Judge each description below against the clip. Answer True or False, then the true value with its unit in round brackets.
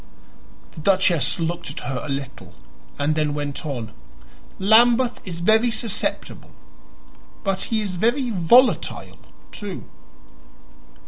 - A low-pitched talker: False (185 Hz)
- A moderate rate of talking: False (115 wpm)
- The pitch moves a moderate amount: False (6.8 semitones)